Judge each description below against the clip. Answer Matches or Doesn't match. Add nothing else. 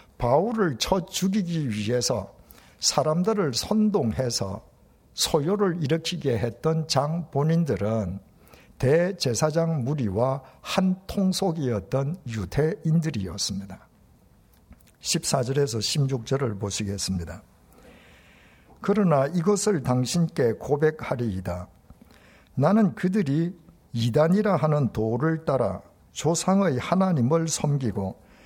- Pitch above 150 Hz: Doesn't match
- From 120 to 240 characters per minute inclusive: Matches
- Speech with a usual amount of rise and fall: Doesn't match